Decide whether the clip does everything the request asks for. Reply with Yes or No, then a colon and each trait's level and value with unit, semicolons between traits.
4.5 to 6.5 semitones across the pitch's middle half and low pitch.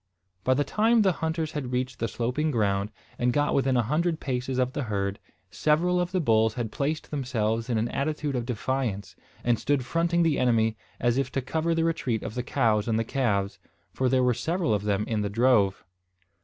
Yes: average, 5.1 semitones; low, 125 Hz